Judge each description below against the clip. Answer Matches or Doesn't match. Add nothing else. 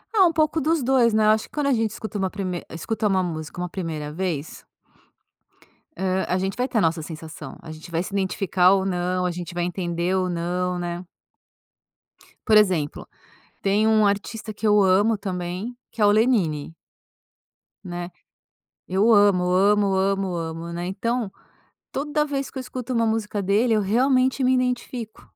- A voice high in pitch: Matches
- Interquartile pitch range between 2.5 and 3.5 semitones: Doesn't match